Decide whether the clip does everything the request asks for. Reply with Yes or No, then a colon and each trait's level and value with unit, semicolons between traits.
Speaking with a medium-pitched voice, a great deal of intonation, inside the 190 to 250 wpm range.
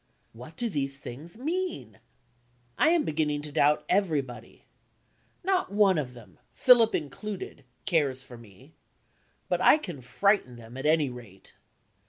No: medium, 150 Hz; wide, 8.1 semitones; average, 140 wpm